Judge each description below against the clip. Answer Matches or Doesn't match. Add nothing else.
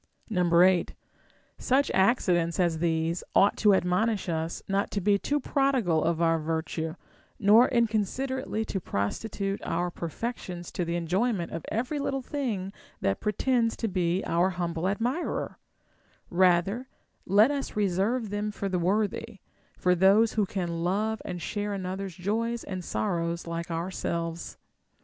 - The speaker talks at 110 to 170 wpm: Matches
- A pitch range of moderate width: Matches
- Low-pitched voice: Doesn't match